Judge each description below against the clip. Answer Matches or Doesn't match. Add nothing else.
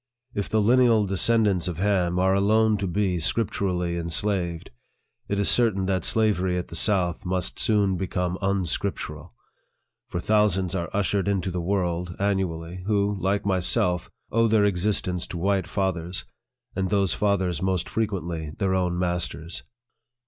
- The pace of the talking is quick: Doesn't match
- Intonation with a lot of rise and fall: Doesn't match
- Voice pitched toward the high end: Doesn't match